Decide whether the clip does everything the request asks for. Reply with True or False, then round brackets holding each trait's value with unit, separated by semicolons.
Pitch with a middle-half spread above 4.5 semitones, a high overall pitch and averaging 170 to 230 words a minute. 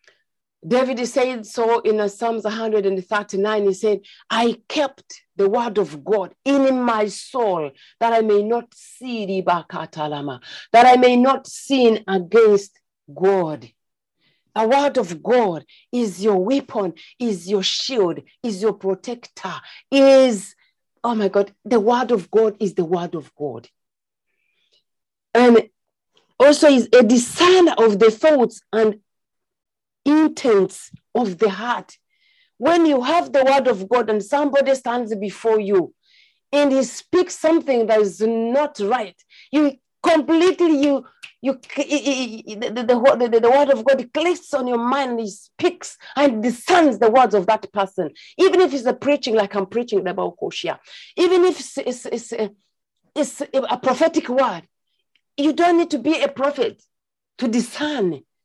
False (5.0 semitones; 235 Hz; 145 wpm)